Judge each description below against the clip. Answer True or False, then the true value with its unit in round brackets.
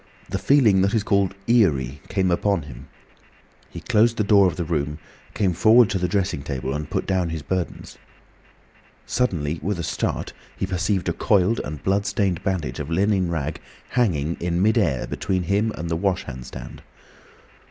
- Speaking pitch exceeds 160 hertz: False (90 Hz)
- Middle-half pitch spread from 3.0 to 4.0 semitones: False (4.6 semitones)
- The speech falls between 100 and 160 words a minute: False (180 wpm)